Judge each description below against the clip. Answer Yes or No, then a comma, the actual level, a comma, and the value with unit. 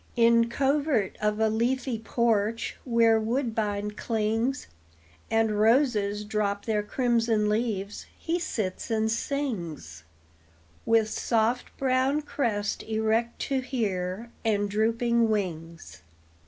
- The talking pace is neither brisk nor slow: No, slow, 105 wpm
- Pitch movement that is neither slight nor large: No, narrow, 2.3 semitones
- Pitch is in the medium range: No, high, 225 Hz